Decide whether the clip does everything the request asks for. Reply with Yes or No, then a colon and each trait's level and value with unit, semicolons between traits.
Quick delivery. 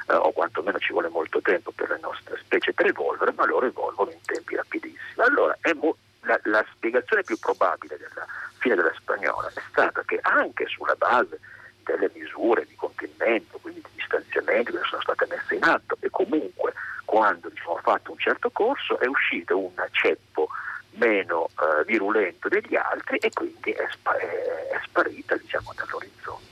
Yes: fast, 175 wpm